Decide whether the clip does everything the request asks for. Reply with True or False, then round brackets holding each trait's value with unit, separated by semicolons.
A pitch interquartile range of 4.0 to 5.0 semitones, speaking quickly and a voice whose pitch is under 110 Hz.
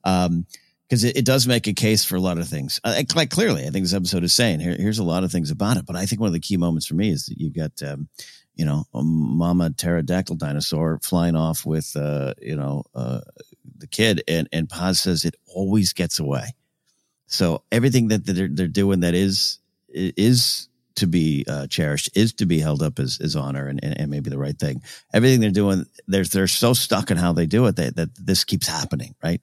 True (4.5 semitones; 230 wpm; 90 Hz)